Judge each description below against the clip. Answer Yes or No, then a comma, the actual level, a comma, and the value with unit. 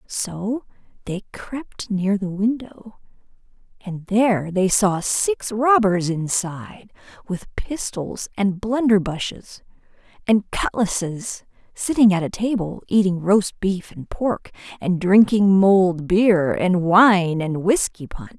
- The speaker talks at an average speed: No, slow, 120 wpm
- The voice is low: No, high, 200 Hz